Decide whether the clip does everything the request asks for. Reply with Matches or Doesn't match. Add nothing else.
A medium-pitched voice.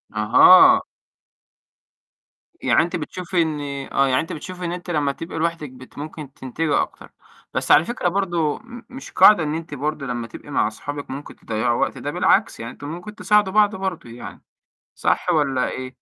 Matches